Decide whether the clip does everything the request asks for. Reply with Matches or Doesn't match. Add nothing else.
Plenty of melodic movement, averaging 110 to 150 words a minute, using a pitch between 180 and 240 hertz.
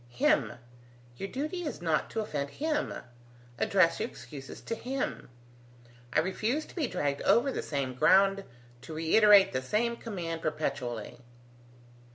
Matches